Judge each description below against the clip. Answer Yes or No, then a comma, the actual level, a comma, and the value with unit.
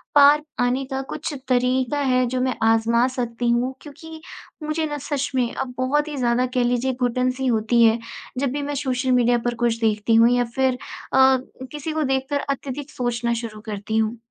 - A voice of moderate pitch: No, very high, 255 Hz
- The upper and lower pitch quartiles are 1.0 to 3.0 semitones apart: Yes, narrow, 2.6 semitones